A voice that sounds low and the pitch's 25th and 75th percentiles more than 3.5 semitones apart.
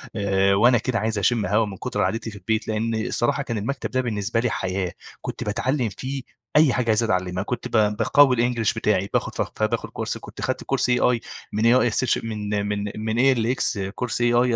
No: low, 115 Hz; average, 3.0 semitones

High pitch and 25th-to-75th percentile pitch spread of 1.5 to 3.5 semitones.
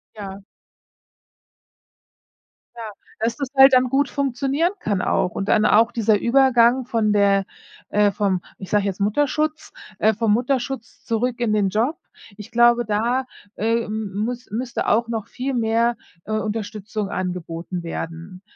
Yes: high, 225 Hz; average, 3.2 semitones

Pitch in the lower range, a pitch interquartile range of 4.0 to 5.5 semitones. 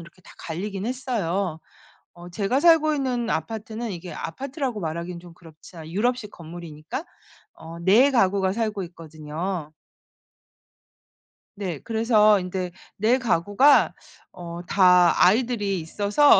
No: high, 195 Hz; average, 5.2 semitones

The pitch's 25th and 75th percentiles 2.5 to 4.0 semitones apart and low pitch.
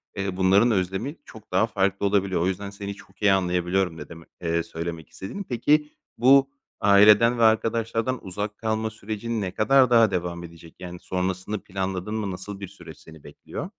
Yes: average, 3.3 semitones; low, 100 Hz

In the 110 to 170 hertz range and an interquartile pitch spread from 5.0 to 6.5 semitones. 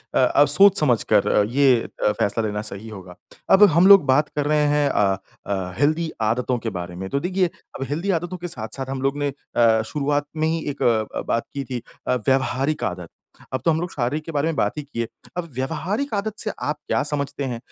Yes: medium, 140 Hz; wide, 5.6 semitones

